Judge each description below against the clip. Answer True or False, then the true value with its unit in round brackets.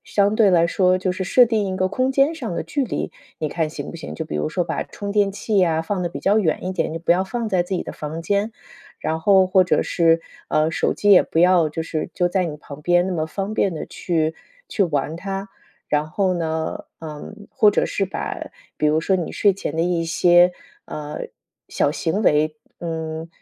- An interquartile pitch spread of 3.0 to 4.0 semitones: True (3.6 semitones)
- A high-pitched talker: False (175 Hz)